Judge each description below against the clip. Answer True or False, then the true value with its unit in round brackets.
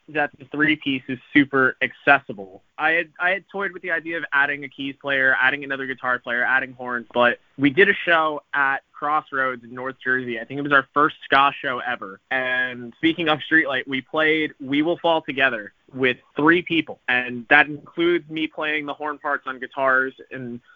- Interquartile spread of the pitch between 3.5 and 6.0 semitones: False (3.0 semitones)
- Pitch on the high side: False (140 Hz)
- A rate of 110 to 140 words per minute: False (200 wpm)